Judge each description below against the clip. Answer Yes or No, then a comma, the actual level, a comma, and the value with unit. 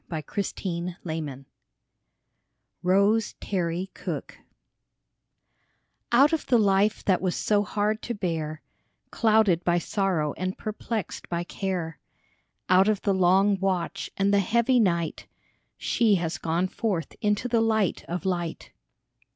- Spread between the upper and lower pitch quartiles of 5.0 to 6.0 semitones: No, average, 3.6 semitones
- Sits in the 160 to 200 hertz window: Yes, high, 190 Hz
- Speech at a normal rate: No, slow, 130 wpm